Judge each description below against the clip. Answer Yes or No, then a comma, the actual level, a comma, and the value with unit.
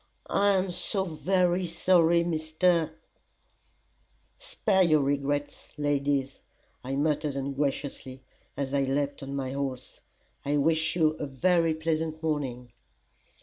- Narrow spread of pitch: No, average, 3.4 semitones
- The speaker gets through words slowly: Yes, slow, 120 wpm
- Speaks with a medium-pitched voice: Yes, medium, 150 Hz